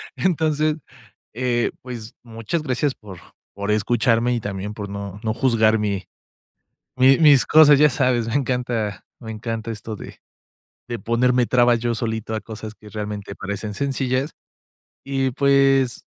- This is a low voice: Yes, low, 120 Hz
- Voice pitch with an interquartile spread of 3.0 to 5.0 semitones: Yes, average, 3.6 semitones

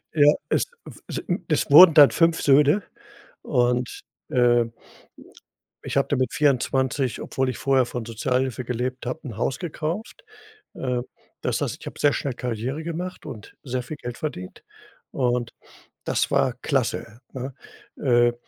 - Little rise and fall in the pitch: No, average, 3.3 semitones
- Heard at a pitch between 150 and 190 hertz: No, low, 130 Hz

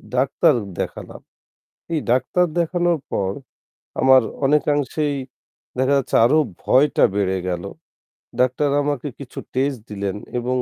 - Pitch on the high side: No, low, 135 Hz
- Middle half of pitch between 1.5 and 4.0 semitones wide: Yes, average, 3.3 semitones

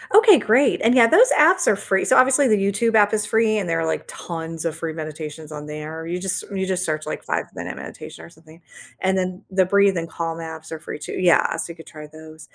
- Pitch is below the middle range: No, medium, 180 Hz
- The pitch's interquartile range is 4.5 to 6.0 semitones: Yes, average, 4.8 semitones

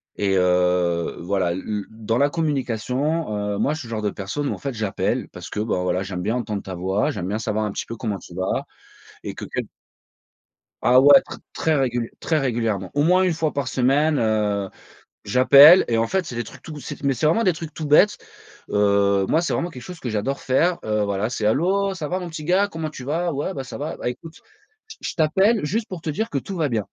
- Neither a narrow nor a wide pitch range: No, wide, 7.2 semitones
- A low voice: Yes, low, 130 Hz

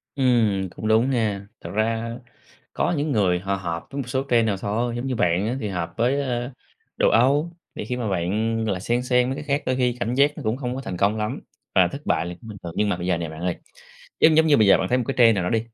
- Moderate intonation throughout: Yes, average, 4.5 semitones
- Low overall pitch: Yes, low, 115 Hz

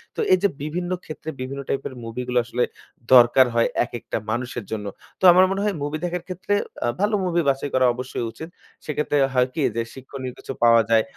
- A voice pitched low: Yes, low, 130 Hz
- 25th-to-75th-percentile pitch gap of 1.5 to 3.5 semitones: No, wide, 5.6 semitones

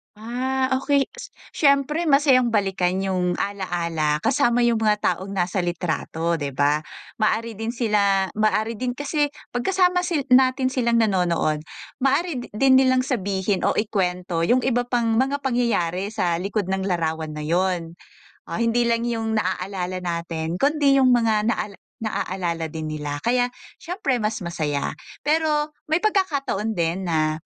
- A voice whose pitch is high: Yes, high, 215 Hz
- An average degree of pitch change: No, wide, 6.4 semitones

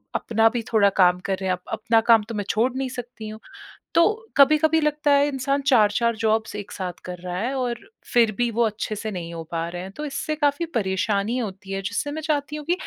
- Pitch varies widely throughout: Yes, wide, 5.7 semitones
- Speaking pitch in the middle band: No, high, 225 Hz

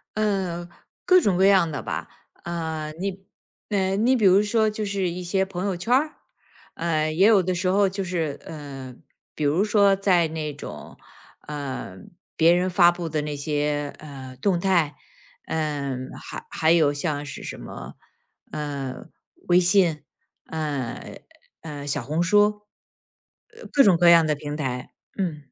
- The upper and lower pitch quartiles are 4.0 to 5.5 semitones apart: Yes, average, 4.6 semitones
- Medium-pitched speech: Yes, medium, 170 Hz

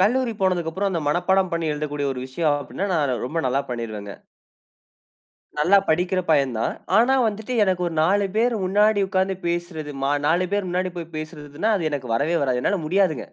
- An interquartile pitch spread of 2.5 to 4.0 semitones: No, average, 4.7 semitones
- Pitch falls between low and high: Yes, medium, 170 Hz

